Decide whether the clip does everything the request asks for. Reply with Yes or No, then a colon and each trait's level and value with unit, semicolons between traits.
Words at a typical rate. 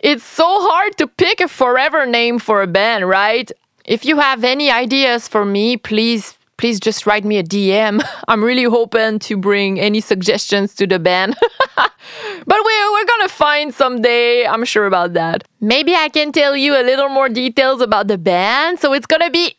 Yes: average, 190 wpm